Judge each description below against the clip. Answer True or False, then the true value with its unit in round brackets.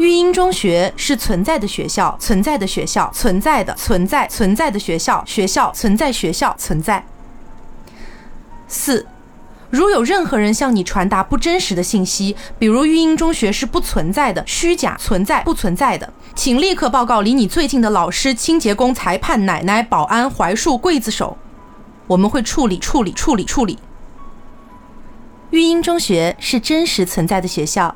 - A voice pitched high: True (220 Hz)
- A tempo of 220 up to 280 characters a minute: True (250 characters per minute)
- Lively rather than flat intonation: True (8.3 semitones)